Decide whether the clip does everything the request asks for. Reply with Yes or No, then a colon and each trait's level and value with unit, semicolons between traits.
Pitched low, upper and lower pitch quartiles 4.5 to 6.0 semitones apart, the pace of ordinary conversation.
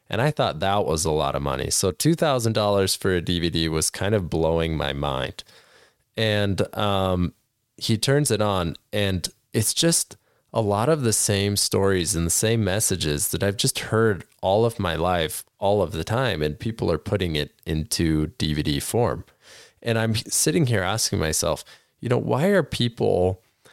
Yes: low, 100 Hz; wide, 5.4 semitones; average, 175 wpm